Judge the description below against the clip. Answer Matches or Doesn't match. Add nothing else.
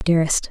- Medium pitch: Matches